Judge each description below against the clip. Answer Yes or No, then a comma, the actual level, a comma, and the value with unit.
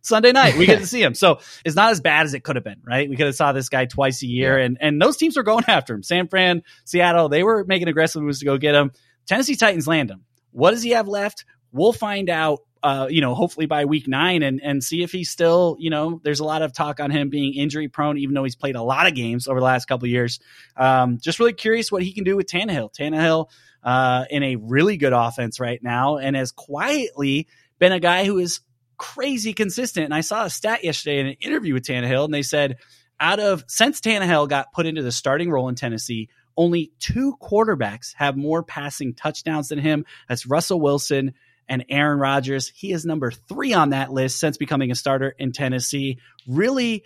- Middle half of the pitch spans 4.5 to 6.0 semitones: Yes, average, 5.1 semitones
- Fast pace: Yes, fast, 230 wpm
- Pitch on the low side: No, medium, 150 Hz